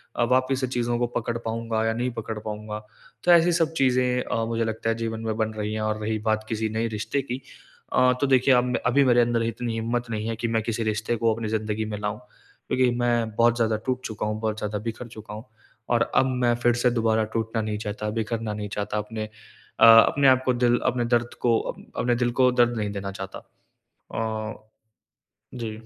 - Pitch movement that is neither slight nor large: No, narrow, 1.9 semitones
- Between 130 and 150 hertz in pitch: No, low, 115 Hz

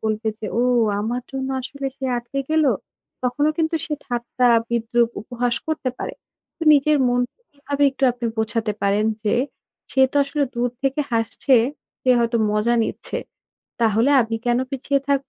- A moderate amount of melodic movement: Yes, average, 3.2 semitones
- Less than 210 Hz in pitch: No, high, 245 Hz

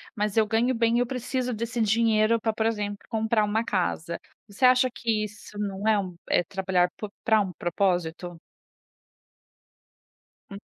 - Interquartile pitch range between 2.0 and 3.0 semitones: Yes, average, 2.7 semitones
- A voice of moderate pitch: No, high, 215 Hz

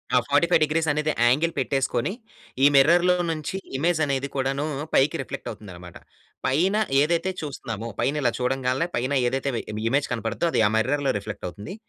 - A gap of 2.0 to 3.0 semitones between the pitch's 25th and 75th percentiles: No, average, 3.9 semitones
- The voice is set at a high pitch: No, medium, 140 Hz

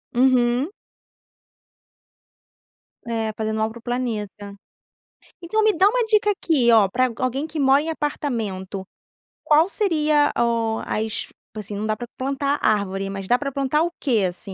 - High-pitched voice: Yes, high, 245 Hz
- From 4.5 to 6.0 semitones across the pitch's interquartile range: Yes, wide, 5.5 semitones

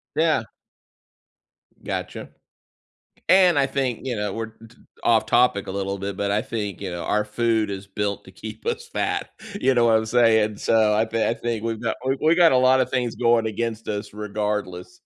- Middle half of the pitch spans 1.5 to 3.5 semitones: Yes, average, 2.9 semitones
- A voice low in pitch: Yes, low, 110 Hz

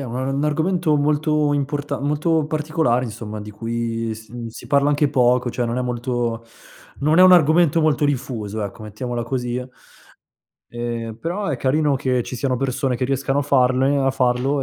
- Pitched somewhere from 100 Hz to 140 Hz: Yes, low, 135 Hz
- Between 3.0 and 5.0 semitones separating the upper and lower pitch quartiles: Yes, average, 3.5 semitones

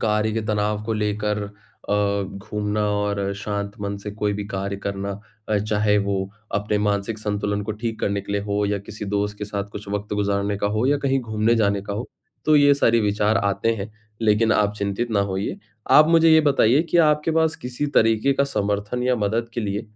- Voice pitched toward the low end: Yes, low, 105 Hz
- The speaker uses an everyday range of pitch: No, narrow, 1.8 semitones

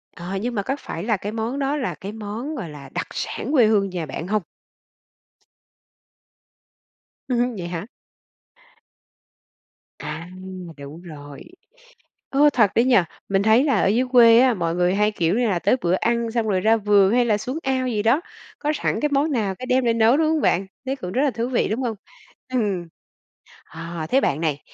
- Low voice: No, high, 220 Hz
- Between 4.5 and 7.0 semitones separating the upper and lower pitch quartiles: Yes, wide, 5.6 semitones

